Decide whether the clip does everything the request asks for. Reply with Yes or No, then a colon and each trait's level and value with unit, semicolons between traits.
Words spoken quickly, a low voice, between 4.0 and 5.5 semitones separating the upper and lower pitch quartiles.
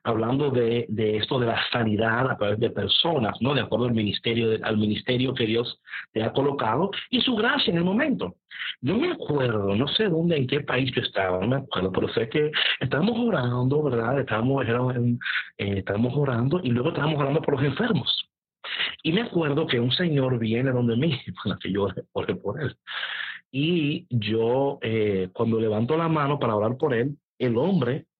Yes: fast, 195 wpm; low, 125 Hz; average, 4.8 semitones